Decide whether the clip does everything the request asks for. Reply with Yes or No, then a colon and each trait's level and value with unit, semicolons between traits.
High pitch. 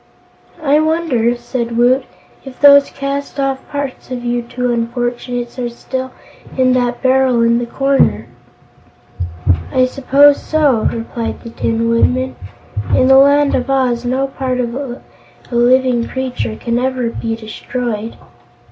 Yes: very high, 255 Hz